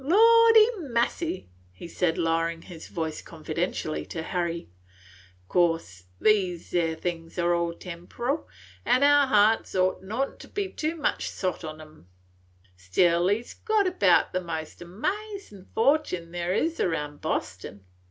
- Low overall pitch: No, medium, 180 Hz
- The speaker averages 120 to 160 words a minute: Yes, average, 140 wpm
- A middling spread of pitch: No, wide, 8.8 semitones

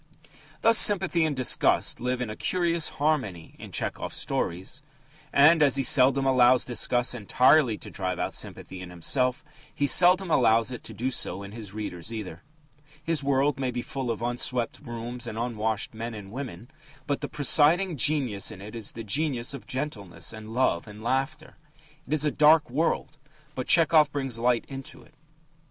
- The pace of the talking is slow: No, average, 175 wpm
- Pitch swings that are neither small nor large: Yes, average, 4.8 semitones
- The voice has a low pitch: Yes, low, 125 Hz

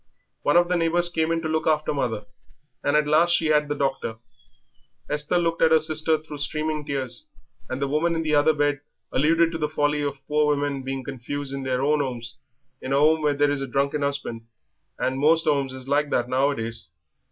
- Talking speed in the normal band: No, fast, 210 wpm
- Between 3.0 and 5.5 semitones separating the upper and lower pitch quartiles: No, narrow, 2.4 semitones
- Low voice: No, medium, 145 Hz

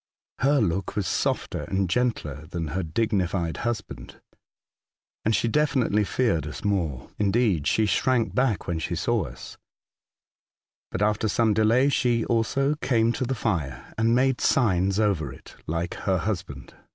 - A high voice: No, low, 105 Hz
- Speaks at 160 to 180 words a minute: No, average, 150 wpm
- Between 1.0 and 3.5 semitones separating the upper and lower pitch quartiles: No, wide, 5.4 semitones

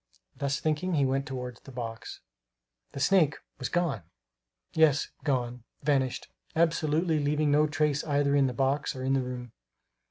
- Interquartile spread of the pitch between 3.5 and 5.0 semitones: No, average, 2.7 semitones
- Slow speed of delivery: No, average, 155 wpm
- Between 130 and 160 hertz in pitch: Yes, medium, 140 Hz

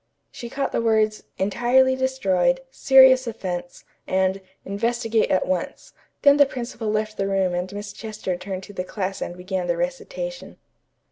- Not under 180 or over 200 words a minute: No, average, 155 wpm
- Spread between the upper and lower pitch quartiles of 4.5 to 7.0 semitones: Yes, average, 4.9 semitones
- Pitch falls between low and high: No, high, 215 Hz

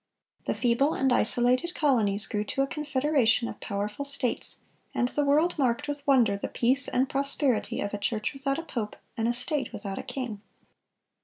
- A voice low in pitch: No, very high, 255 Hz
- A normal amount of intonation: Yes, average, 3.8 semitones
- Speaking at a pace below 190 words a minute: Yes, average, 180 wpm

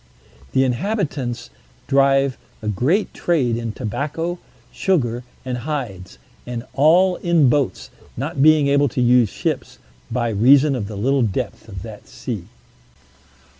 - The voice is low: Yes, low, 130 Hz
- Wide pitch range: No, average, 4.1 semitones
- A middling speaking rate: No, slow, 130 wpm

